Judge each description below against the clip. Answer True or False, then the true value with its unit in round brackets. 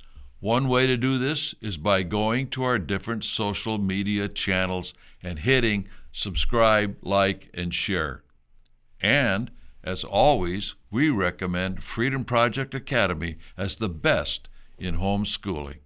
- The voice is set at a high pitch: False (100 Hz)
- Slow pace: True (125 wpm)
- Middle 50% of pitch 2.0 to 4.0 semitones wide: False (4.4 semitones)